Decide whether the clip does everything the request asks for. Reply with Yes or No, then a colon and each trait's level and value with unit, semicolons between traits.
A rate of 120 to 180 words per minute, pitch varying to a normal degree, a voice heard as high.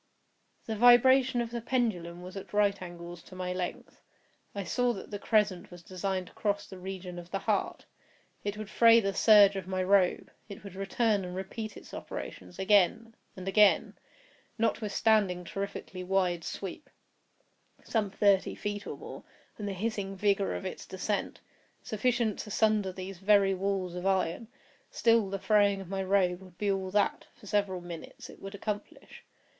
No: average, 165 wpm; narrow, 2.3 semitones; high, 195 Hz